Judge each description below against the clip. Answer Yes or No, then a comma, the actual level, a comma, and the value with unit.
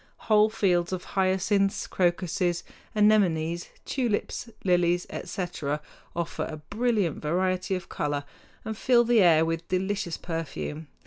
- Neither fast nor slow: No, slow, 120 wpm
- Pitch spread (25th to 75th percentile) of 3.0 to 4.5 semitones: Yes, average, 3.5 semitones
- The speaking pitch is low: No, medium, 180 Hz